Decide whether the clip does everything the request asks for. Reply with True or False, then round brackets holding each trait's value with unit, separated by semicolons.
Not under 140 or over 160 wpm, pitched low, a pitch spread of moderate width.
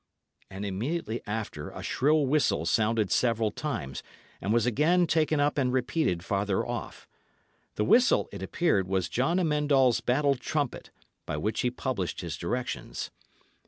False (150 wpm; 120 Hz; 6.8 semitones)